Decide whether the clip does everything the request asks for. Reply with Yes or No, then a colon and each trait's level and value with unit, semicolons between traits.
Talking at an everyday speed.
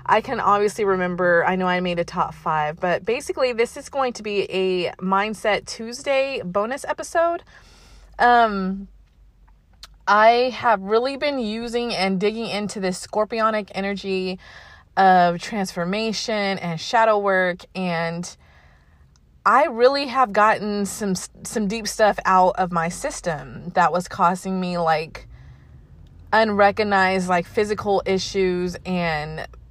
No: slow, 125 wpm